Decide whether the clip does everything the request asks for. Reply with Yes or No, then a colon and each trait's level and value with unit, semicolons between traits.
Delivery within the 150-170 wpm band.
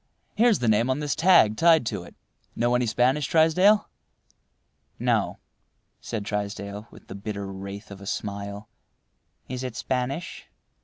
No: average, 140 wpm